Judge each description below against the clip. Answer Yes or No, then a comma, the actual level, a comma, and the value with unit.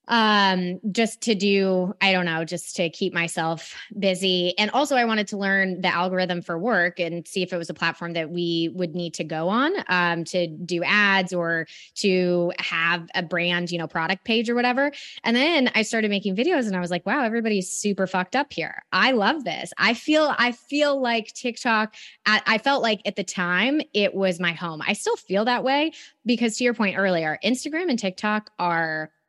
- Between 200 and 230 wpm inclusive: Yes, fast, 205 wpm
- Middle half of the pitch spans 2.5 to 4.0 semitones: No, average, 4.8 semitones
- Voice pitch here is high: Yes, high, 195 Hz